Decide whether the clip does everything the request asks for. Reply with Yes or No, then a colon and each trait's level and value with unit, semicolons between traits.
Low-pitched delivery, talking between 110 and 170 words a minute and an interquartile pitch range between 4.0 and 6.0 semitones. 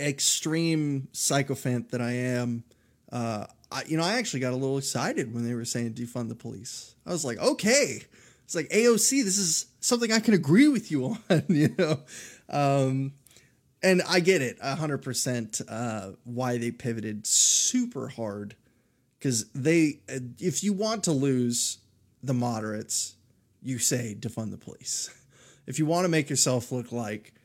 Yes: low, 130 Hz; average, 165 wpm; average, 4.8 semitones